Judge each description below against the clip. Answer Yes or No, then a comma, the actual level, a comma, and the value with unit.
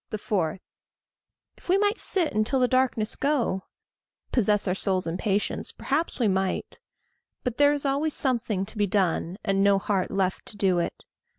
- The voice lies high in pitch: Yes, high, 210 Hz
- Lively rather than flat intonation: Yes, wide, 5.8 semitones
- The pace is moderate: Yes, average, 170 wpm